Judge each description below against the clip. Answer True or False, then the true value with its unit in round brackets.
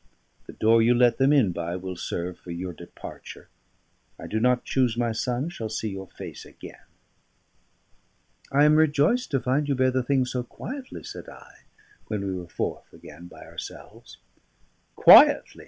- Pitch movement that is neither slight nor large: False (6.4 semitones)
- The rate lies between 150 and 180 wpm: True (170 wpm)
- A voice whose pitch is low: True (120 Hz)